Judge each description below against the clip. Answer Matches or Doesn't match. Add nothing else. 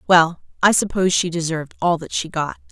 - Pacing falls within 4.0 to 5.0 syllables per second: Doesn't match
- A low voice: Doesn't match